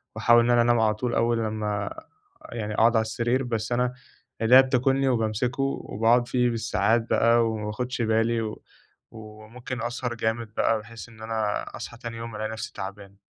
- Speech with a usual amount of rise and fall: No, narrow, 1.6 semitones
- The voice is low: Yes, low, 115 Hz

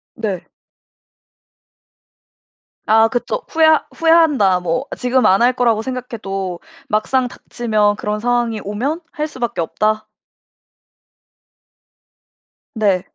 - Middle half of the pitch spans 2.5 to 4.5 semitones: Yes, average, 3.6 semitones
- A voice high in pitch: Yes, high, 225 Hz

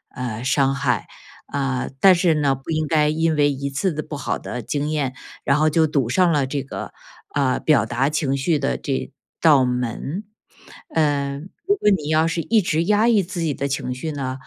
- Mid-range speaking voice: Yes, medium, 145 Hz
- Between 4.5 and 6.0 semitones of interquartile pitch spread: No, average, 3.3 semitones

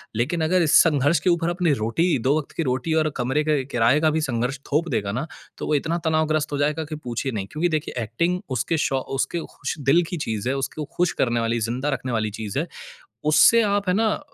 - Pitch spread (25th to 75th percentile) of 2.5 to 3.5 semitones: No, average, 5.0 semitones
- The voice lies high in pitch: No, medium, 150 Hz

